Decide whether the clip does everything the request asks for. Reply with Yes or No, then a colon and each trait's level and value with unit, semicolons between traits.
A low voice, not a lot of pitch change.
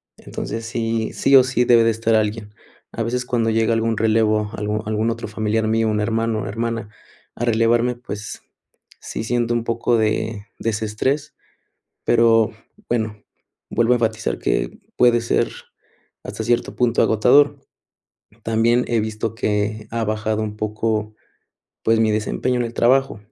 Yes: low, 115 Hz; narrow, 1.5 semitones